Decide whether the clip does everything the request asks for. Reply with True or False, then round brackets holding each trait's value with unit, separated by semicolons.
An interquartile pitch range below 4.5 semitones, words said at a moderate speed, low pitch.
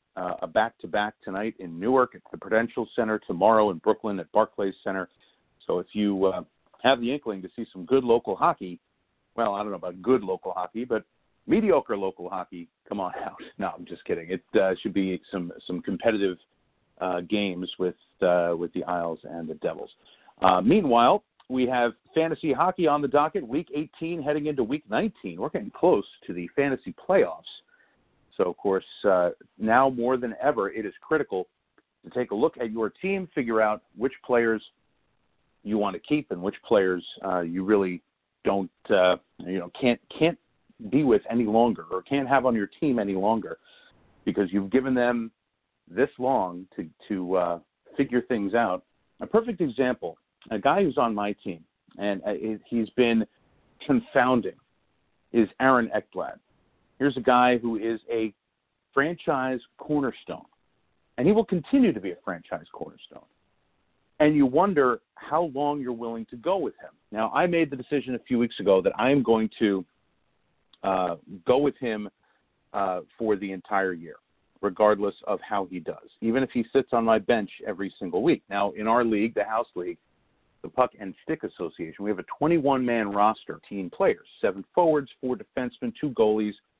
False (5.1 semitones; 175 wpm; 115 Hz)